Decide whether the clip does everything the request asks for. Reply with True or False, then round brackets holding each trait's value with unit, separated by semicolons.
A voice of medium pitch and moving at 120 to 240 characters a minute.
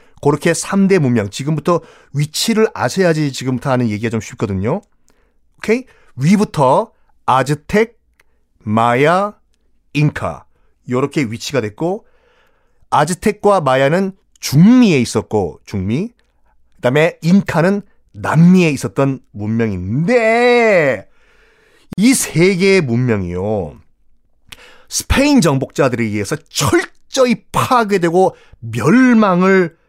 True (150 Hz; 225 characters per minute)